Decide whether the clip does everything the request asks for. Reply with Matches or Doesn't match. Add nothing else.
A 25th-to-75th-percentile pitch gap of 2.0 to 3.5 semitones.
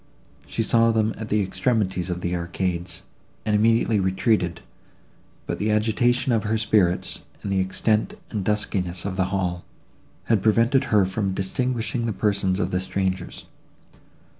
Matches